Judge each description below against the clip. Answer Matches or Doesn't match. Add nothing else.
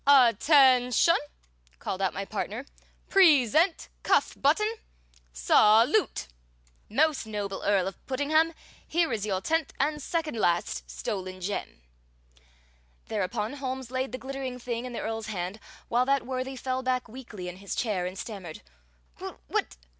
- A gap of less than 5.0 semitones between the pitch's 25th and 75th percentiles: Doesn't match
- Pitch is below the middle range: Doesn't match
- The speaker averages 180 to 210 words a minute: Doesn't match